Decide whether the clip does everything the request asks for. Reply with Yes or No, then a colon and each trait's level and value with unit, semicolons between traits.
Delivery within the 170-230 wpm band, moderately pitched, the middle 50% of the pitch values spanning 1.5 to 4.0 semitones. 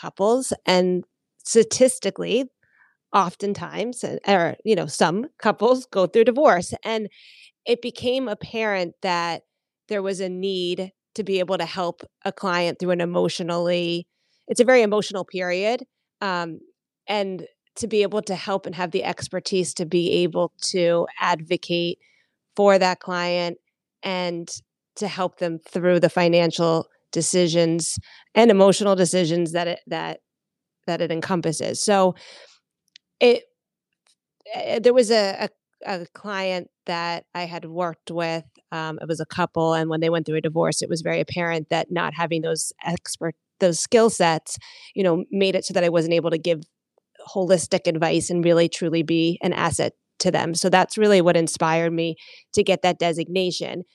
No: average, 155 wpm; medium, 180 Hz; average, 2.8 semitones